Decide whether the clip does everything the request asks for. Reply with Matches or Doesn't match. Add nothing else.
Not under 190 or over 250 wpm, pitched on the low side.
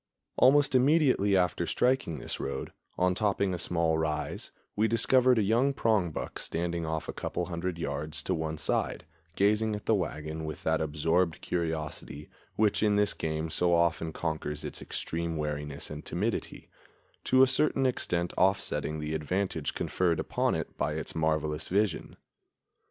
Doesn't match